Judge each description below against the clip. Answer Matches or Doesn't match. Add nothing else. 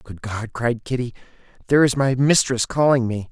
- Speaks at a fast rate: Doesn't match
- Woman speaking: Doesn't match